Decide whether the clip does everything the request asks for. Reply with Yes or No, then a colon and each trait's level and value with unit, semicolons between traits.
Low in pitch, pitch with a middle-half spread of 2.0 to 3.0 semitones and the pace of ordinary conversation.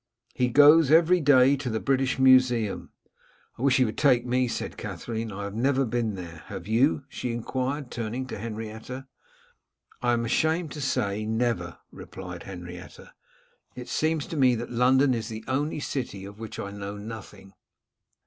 No: low, 120 Hz; average, 3.6 semitones; average, 170 wpm